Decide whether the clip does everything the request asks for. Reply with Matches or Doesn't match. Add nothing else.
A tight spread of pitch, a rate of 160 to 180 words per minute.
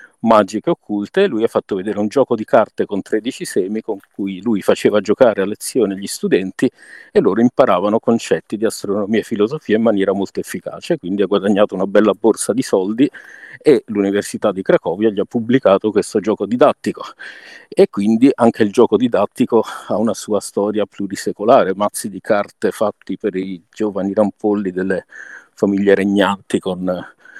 Matches